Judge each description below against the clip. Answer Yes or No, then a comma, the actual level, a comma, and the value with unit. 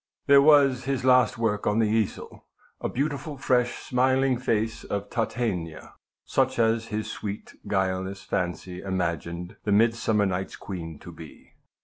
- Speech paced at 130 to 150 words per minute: Yes, average, 140 wpm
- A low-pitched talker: Yes, low, 110 Hz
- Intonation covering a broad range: No, average, 5.0 semitones